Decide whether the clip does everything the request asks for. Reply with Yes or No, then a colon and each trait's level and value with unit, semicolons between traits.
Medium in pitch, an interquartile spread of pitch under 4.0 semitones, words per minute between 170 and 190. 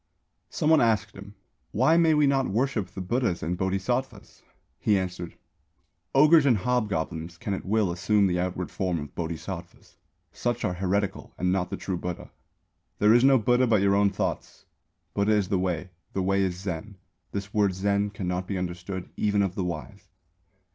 No: low, 100 Hz; average, 3.2 semitones; average, 180 wpm